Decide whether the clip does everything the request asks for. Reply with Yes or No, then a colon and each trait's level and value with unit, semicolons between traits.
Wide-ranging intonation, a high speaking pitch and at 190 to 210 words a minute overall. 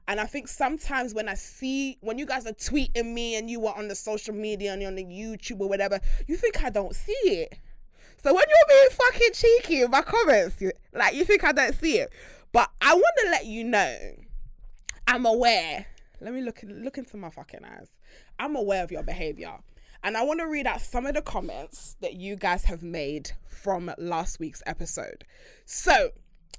Yes: wide, 7.2 semitones; high, 235 Hz; fast, 205 wpm